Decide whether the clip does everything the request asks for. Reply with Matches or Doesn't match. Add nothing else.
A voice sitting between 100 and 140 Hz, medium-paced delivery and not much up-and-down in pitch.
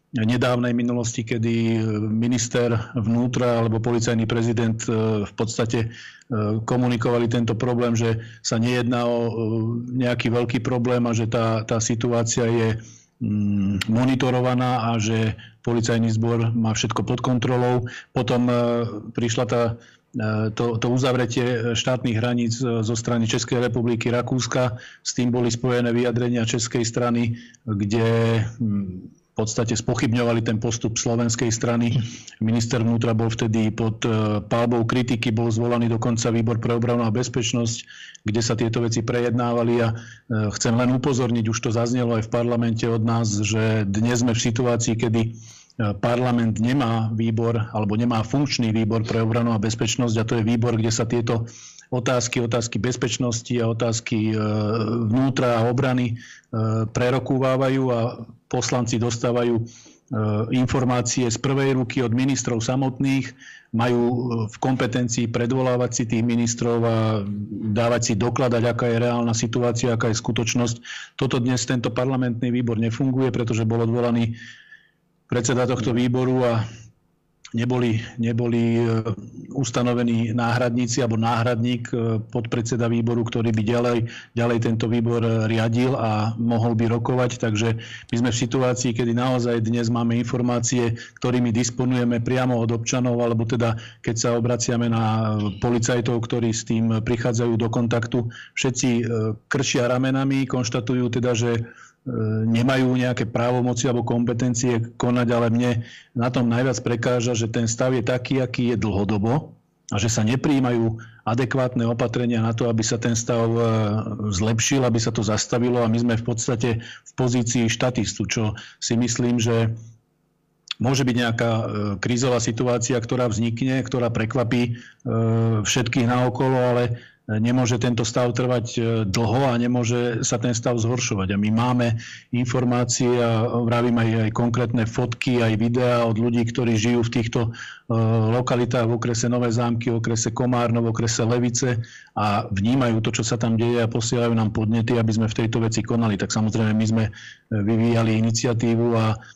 Matches